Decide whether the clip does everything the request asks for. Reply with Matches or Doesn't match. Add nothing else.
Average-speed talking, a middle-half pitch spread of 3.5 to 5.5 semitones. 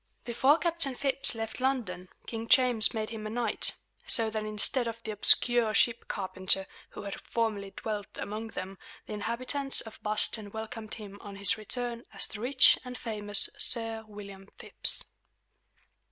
Doesn't match